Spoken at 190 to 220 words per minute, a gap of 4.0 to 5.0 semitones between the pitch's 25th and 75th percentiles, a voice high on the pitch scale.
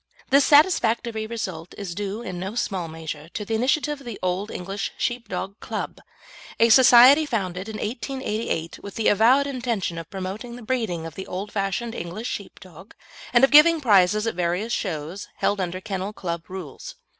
No: average, 170 wpm; average, 4.5 semitones; high, 205 Hz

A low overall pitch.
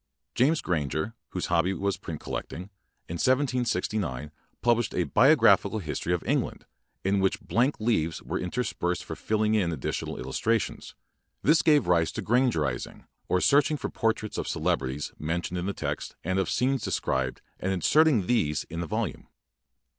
Yes: very low, 95 Hz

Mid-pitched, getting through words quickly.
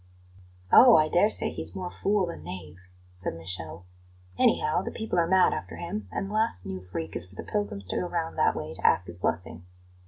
Yes: medium, 160 Hz; fast, 215 wpm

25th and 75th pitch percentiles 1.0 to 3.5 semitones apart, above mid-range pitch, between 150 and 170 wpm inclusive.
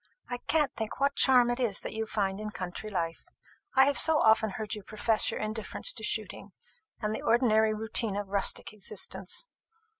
No: average, 2.9 semitones; high, 220 Hz; average, 185 wpm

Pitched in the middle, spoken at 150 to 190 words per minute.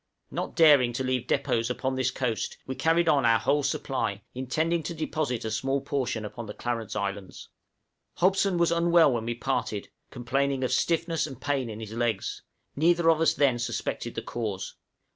No: low, 130 Hz; average, 180 wpm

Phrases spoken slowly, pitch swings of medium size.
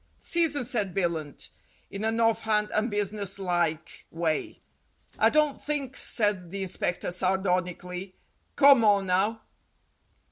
Yes: slow, 120 wpm; average, 3.9 semitones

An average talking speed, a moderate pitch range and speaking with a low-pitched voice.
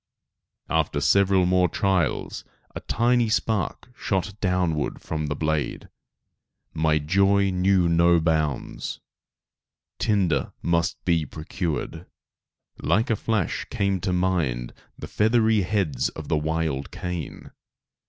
No: slow, 115 wpm; average, 3.9 semitones; very low, 90 Hz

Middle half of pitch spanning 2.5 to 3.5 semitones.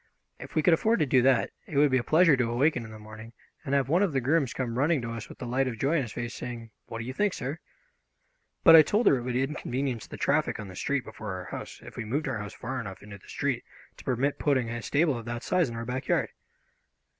No: average, 4.0 semitones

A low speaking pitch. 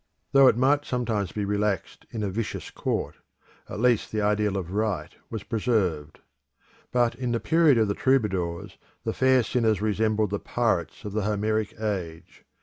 Yes: low, 110 Hz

